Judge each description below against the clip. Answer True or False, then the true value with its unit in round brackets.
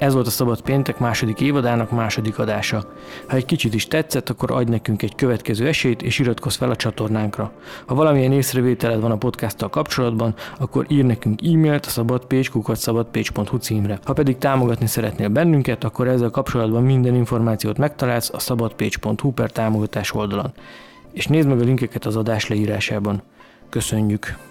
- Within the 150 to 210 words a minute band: True (155 wpm)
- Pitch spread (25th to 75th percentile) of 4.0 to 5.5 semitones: False (3.0 semitones)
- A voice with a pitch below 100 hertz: False (120 Hz)